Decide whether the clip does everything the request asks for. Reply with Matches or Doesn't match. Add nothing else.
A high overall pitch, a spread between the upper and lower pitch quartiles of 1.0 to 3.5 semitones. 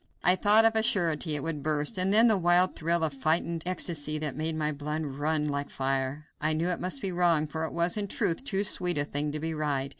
Doesn't match